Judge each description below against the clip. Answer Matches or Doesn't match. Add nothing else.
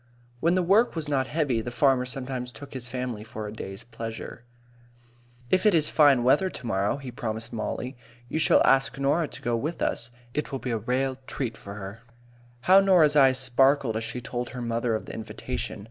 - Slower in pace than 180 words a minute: Doesn't match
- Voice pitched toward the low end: Matches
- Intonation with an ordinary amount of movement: Matches